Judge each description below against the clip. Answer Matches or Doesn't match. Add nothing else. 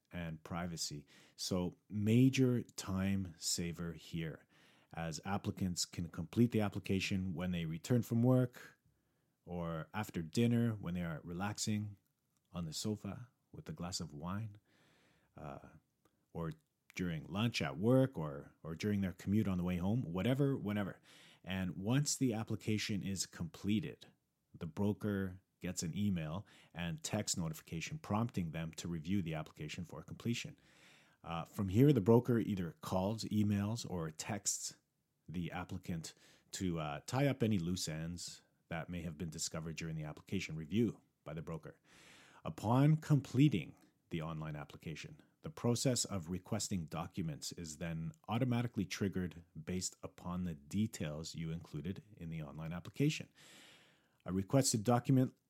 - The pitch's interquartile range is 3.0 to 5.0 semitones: Doesn't match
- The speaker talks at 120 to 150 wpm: Matches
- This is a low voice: Matches